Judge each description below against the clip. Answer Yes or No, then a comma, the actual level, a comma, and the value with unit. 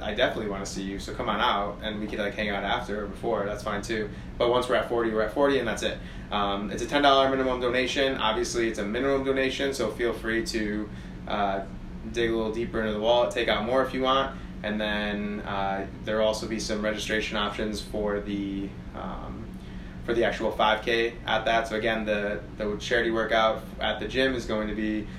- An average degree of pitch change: No, narrow, 2.2 semitones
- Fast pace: Yes, fast, 220 wpm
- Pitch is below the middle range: Yes, low, 110 Hz